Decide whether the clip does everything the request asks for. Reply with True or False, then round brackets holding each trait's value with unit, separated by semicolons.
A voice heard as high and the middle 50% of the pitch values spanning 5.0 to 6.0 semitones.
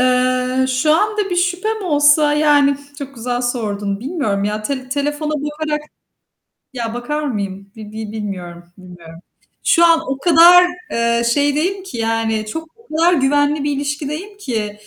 True (275 Hz; 5.4 semitones)